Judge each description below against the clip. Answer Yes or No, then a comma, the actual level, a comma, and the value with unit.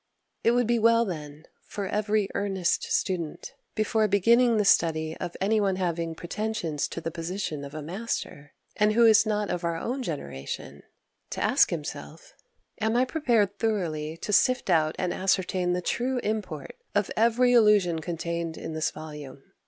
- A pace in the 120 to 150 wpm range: No, average, 165 wpm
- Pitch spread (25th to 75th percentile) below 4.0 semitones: No, average, 5.1 semitones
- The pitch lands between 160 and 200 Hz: Yes, high, 190 Hz